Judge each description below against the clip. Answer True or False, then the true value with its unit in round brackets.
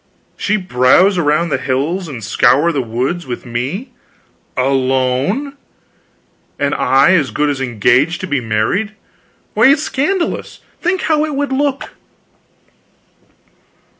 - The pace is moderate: False (125 wpm)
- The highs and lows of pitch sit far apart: True (8.9 semitones)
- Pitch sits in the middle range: True (150 Hz)